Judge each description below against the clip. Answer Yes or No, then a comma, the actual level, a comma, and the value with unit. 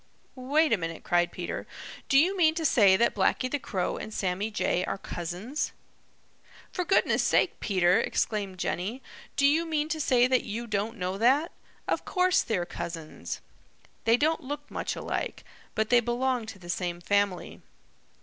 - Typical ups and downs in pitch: No, wide, 7.1 semitones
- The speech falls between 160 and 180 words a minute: Yes, average, 170 wpm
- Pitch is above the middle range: Yes, high, 225 Hz